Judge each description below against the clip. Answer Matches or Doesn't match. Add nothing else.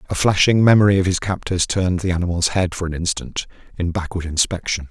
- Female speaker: Doesn't match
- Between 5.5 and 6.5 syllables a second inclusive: Matches